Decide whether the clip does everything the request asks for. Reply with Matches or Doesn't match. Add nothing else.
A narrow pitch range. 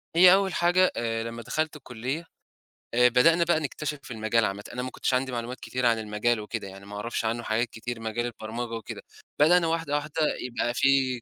Doesn't match